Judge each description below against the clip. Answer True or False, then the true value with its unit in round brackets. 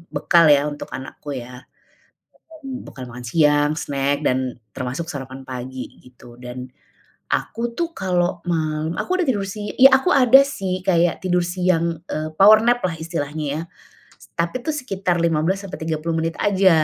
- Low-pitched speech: False (165 Hz)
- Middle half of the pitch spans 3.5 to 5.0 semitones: True (4.5 semitones)